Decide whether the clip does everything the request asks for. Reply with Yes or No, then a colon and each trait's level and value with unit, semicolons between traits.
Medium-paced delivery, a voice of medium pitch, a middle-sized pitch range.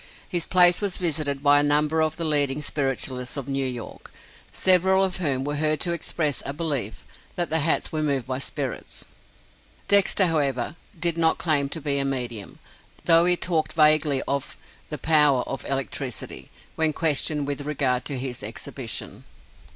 Yes: average, 165 wpm; medium, 150 Hz; average, 3.1 semitones